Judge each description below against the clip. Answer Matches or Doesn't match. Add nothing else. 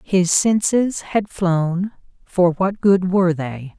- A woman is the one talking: Matches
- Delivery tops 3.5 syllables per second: Doesn't match